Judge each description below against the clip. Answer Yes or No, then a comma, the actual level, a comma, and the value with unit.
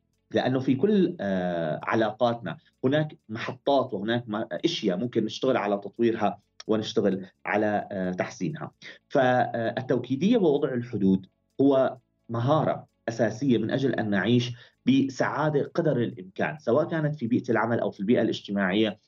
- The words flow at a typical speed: Yes, average, 115 wpm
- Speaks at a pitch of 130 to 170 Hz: No, low, 115 Hz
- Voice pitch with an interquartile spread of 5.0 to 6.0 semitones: Yes, wide, 5.4 semitones